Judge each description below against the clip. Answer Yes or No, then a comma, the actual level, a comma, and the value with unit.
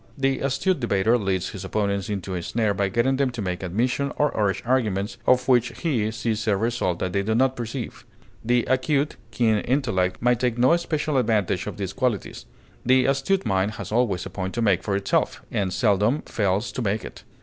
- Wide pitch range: No, average, 4.6 semitones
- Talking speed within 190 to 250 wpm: Yes, average, 200 wpm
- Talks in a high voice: No, low, 115 Hz